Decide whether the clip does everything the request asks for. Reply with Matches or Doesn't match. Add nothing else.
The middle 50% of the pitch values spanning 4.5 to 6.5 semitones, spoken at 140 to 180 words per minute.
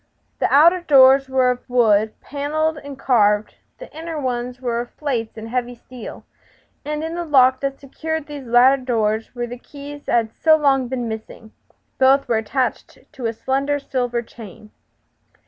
Doesn't match